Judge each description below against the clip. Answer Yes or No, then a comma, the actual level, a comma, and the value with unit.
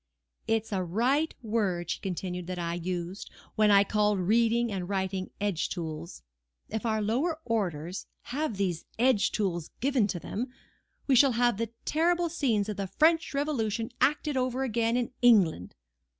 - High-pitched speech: Yes, high, 215 Hz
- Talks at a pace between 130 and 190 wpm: Yes, average, 165 wpm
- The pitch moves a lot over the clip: No, average, 5.0 semitones